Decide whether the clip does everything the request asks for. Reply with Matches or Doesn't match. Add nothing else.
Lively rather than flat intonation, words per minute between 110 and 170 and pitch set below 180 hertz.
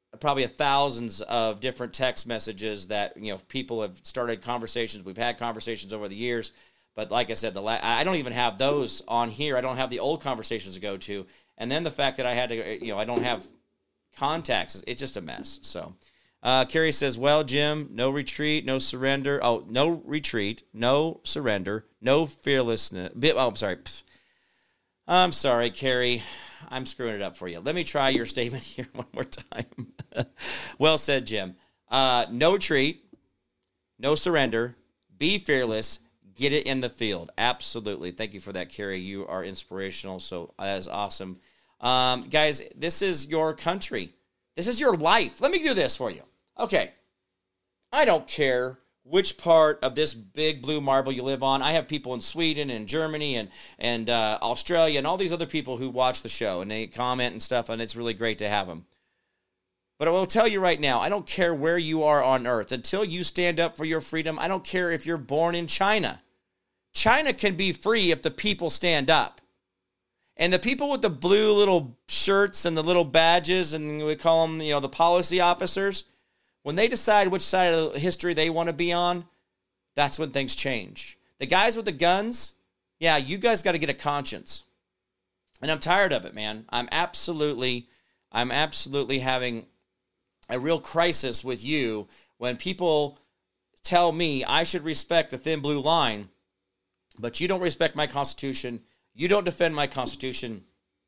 Doesn't match